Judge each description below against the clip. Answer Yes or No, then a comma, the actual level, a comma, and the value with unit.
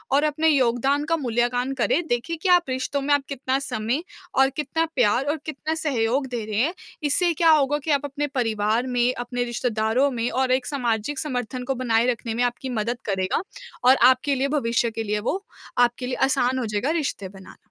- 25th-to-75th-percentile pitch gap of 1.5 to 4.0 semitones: Yes, average, 3.3 semitones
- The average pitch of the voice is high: Yes, very high, 255 Hz